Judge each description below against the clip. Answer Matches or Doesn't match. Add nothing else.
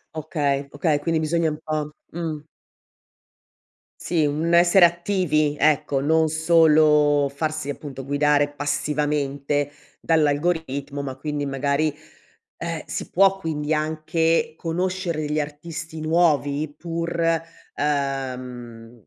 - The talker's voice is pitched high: Doesn't match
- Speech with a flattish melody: Matches